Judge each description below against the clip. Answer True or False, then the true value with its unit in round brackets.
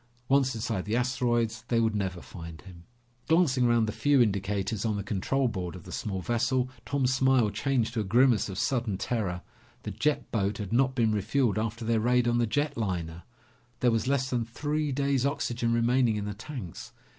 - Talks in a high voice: False (115 Hz)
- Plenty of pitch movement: False (3.9 semitones)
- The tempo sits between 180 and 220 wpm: True (195 wpm)